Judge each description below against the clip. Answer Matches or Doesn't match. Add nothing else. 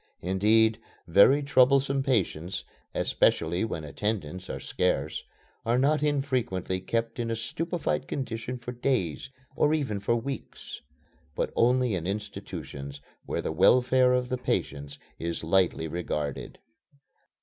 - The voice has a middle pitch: Doesn't match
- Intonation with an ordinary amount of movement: Doesn't match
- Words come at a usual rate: Doesn't match